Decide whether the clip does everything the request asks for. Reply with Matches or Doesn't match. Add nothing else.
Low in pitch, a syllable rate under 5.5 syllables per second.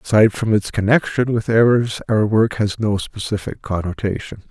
Matches